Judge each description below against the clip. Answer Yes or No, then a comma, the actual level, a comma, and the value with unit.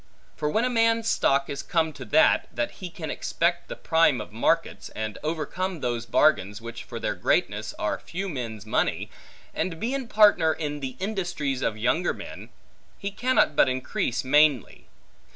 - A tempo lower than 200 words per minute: Yes, average, 170 wpm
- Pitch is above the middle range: No, medium, 155 Hz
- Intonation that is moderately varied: No, wide, 6.4 semitones